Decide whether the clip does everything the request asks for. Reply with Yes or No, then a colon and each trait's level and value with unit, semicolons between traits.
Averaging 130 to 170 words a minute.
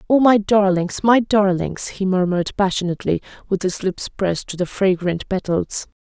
Yes: average, 160 wpm